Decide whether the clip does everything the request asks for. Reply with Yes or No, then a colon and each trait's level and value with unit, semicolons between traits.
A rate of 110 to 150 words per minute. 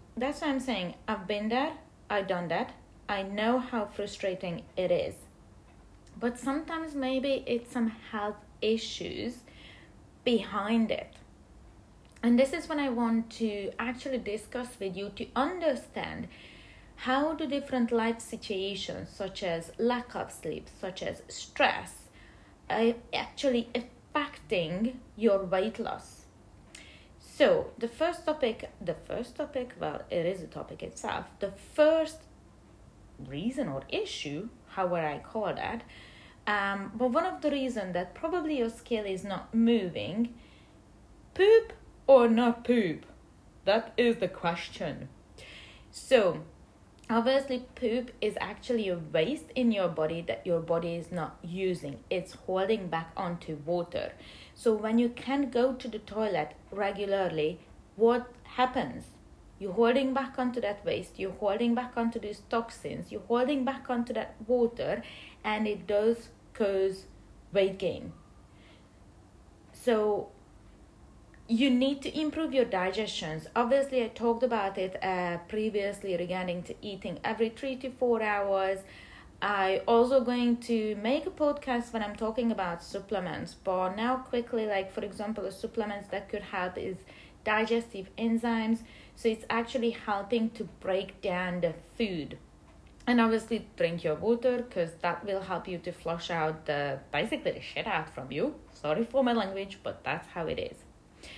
Yes: average, 145 wpm